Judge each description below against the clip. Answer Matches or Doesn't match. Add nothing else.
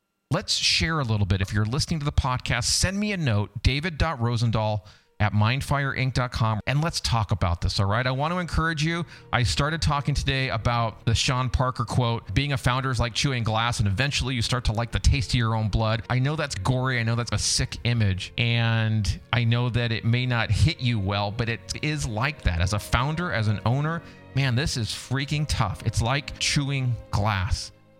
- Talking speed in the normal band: Doesn't match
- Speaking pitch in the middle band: Doesn't match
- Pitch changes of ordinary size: Matches